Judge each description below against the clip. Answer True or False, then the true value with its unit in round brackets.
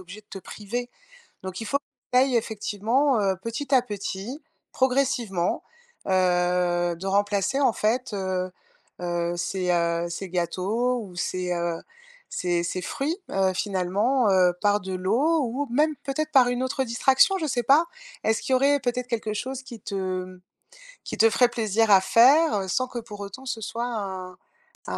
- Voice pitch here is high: True (220 Hz)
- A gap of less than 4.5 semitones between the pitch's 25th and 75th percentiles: False (5.2 semitones)